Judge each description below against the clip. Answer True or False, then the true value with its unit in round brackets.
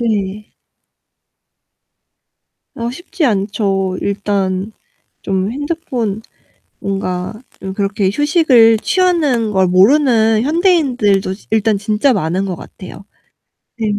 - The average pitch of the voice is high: True (215 Hz)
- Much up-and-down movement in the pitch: False (4.8 semitones)